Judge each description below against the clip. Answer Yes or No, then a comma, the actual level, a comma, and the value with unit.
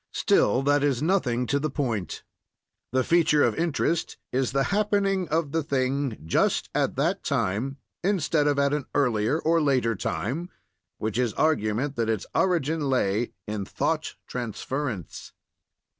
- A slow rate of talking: No, average, 145 wpm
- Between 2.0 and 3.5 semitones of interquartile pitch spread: No, average, 5.0 semitones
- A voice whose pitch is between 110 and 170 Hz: Yes, medium, 140 Hz